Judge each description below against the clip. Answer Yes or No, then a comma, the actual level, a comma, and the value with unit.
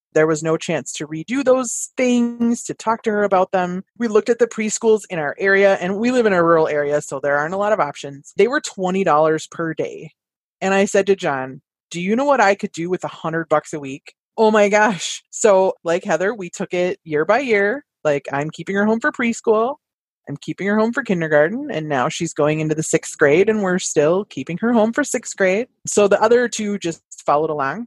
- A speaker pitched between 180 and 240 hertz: Yes, high, 190 Hz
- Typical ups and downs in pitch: No, wide, 5.7 semitones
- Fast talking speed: Yes, fast, 235 wpm